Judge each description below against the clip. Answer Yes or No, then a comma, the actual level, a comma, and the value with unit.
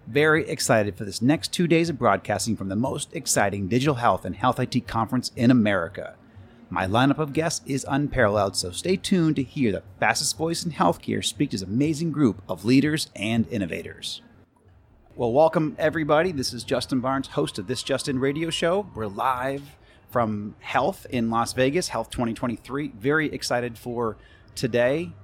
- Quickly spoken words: No, average, 170 wpm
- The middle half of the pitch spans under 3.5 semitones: No, average, 5.1 semitones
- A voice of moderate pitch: No, low, 125 Hz